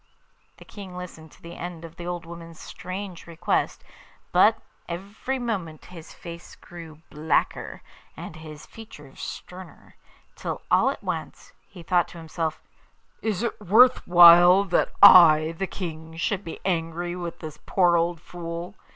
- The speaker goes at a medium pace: Yes, average, 150 wpm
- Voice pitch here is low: No, medium, 170 Hz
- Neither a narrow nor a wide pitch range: No, narrow, 1.9 semitones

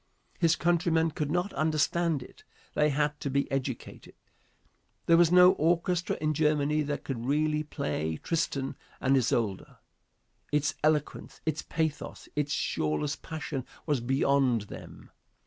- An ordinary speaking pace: No, slow, 130 wpm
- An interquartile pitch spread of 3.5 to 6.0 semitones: No, average, 2.9 semitones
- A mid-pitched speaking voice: Yes, medium, 150 Hz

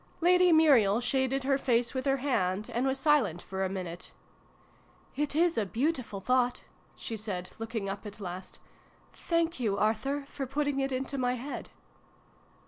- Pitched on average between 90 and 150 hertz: No, very high, 255 Hz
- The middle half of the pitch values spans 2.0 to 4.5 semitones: No, average, 5.1 semitones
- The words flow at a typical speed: Yes, average, 170 wpm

